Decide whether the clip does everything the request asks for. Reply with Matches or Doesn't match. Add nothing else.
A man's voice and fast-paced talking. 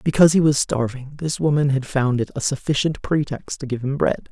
Matches